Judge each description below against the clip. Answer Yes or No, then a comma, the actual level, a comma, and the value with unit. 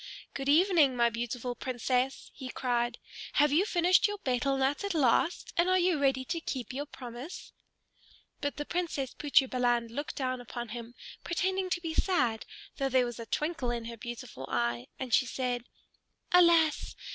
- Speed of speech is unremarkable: Yes, average, 170 wpm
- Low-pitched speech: No, very high, 265 Hz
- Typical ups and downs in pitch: Yes, average, 5.0 semitones